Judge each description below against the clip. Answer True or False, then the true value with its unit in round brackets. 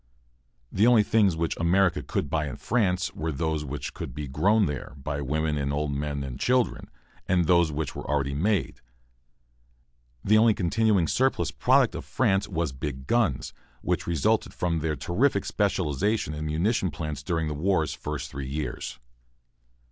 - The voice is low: True (80 Hz)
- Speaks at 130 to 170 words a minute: True (165 wpm)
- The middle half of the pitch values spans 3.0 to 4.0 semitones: False (5.0 semitones)